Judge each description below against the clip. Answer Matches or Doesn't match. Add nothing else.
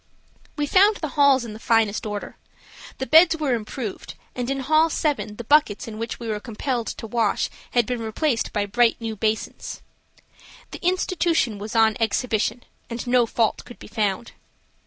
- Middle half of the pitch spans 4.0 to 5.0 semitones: Matches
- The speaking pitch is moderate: Doesn't match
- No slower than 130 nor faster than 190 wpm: Matches